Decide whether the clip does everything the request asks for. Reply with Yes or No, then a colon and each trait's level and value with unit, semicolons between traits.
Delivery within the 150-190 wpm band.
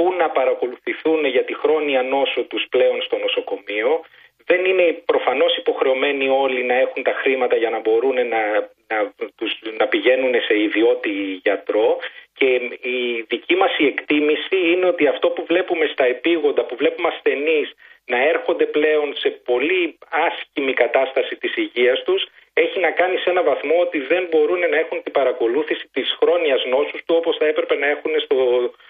Yes: average, 160 wpm